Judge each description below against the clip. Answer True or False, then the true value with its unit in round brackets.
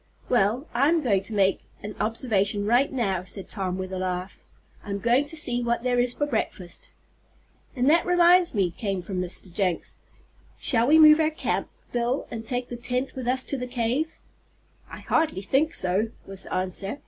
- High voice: True (235 Hz)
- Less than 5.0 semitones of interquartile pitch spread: False (5.5 semitones)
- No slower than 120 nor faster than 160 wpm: False (185 wpm)